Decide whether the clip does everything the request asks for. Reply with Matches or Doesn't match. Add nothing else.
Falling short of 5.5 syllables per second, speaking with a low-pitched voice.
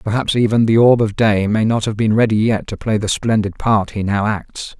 Matches